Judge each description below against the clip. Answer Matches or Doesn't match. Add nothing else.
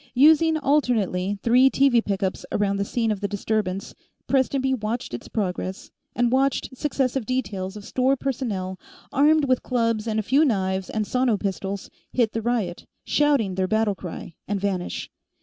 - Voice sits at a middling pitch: Doesn't match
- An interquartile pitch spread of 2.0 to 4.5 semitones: Doesn't match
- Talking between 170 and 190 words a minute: Doesn't match